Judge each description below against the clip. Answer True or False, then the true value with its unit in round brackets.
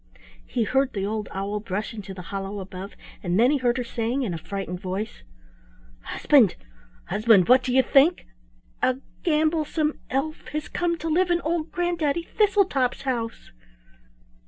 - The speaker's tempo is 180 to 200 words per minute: False (160 wpm)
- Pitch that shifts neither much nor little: False (7.2 semitones)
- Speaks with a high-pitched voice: True (250 Hz)